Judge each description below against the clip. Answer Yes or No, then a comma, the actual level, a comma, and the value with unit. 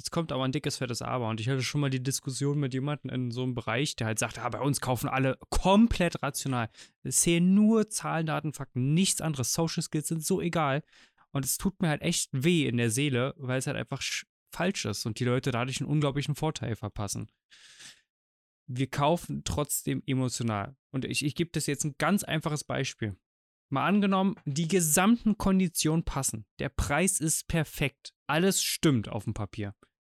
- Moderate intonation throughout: Yes, average, 4.6 semitones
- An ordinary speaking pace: No, fast, 195 wpm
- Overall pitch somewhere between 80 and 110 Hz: No, medium, 140 Hz